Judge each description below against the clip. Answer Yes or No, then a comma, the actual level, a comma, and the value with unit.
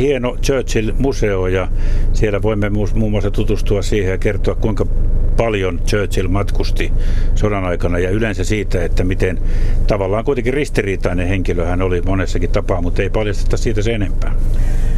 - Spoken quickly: No, average, 145 wpm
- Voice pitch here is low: Yes, low, 100 Hz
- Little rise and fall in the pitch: Yes, narrow, 2.1 semitones